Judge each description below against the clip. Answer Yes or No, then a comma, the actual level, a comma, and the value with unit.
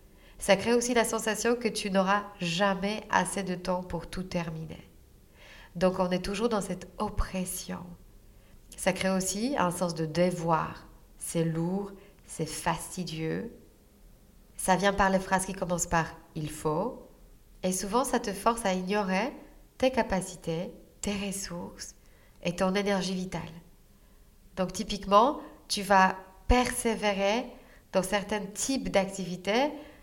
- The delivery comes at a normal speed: No, slow, 135 wpm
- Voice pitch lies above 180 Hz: Yes, high, 190 Hz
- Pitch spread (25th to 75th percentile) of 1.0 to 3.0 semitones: Yes, average, 2.7 semitones